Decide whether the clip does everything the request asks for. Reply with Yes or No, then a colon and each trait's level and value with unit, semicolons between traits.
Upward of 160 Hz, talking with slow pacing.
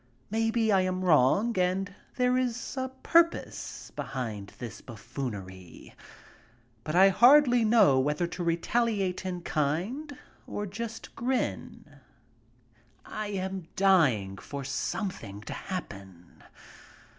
Yes: medium, 185 Hz; slow, 110 wpm